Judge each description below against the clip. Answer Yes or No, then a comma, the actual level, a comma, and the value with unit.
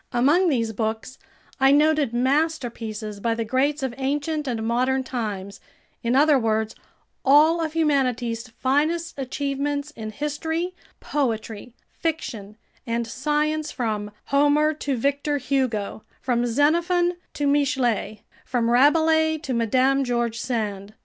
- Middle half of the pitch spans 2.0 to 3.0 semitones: No, average, 4.4 semitones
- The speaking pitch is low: No, very high, 265 Hz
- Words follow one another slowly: Yes, slow, 125 wpm